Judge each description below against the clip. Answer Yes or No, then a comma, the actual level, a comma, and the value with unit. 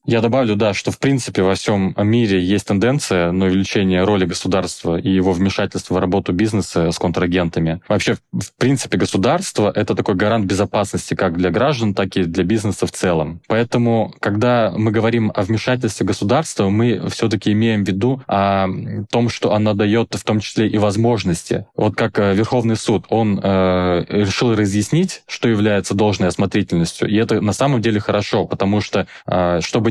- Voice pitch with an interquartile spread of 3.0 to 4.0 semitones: Yes, average, 3.3 semitones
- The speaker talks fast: Yes, fast, 165 wpm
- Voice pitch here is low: Yes, low, 105 Hz